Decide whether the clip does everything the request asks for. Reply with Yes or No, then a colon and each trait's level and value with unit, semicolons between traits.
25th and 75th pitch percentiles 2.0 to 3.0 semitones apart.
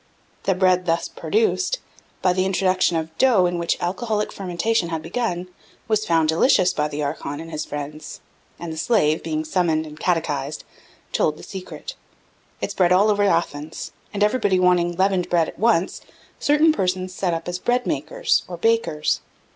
No: average, 3.8 semitones